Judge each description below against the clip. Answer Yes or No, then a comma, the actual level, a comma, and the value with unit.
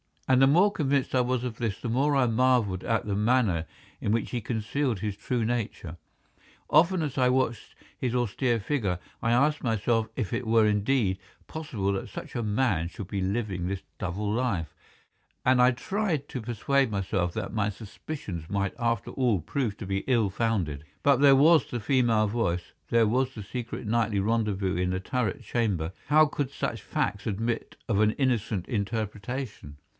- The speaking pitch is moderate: No, low, 115 Hz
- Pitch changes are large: No, average, 4.2 semitones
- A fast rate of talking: No, average, 175 wpm